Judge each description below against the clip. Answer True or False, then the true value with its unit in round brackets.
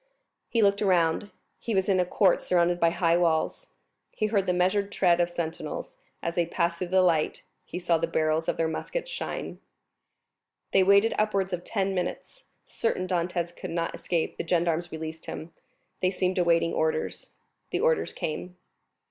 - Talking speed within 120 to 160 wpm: False (175 wpm)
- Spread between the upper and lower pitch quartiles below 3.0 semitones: True (2.4 semitones)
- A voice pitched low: False (175 Hz)